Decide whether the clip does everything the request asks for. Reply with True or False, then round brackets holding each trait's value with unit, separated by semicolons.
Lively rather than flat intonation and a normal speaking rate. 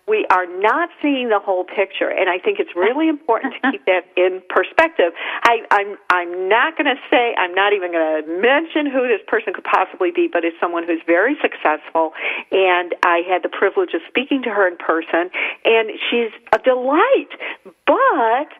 True (7.8 semitones; 185 wpm)